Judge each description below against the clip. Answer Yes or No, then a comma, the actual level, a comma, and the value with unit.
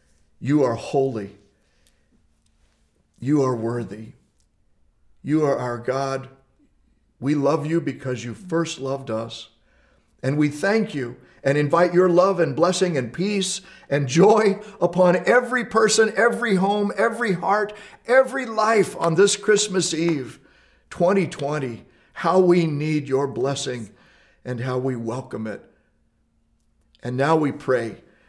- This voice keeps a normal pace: No, slow, 125 wpm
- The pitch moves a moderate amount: No, wide, 7.3 semitones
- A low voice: No, medium, 145 Hz